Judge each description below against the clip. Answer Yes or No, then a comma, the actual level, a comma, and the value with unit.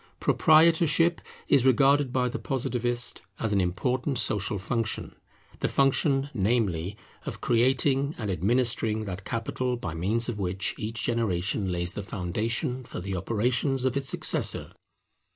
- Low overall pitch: Yes, low, 115 Hz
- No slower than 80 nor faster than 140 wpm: Yes, slow, 135 wpm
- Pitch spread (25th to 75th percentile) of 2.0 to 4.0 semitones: No, average, 4.8 semitones